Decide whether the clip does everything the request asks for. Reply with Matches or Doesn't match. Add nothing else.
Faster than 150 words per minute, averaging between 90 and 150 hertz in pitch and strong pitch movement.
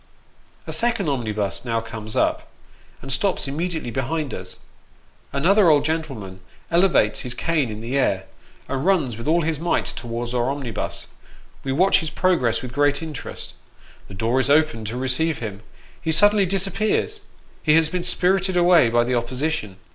Matches